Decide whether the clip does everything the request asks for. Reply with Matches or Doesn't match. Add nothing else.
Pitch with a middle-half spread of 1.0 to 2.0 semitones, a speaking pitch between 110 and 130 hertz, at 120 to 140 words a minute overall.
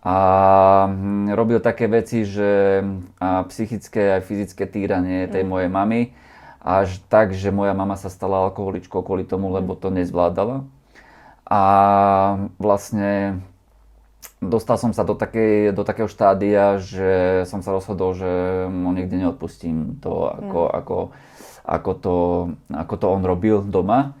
Doesn't match